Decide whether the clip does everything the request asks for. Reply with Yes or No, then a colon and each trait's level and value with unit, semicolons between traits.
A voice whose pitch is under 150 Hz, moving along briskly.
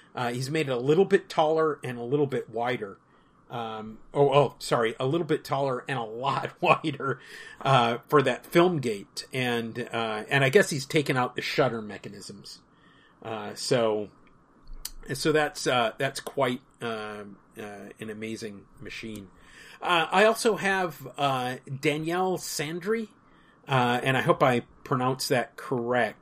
No: low, 135 Hz; average, 155 wpm